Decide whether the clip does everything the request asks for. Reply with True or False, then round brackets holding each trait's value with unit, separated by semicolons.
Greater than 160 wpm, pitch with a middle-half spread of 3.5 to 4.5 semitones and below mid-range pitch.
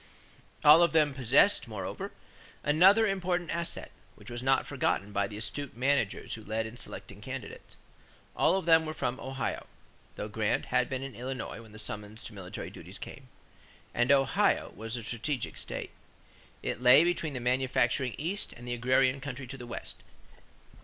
True (170 wpm; 4.1 semitones; 130 Hz)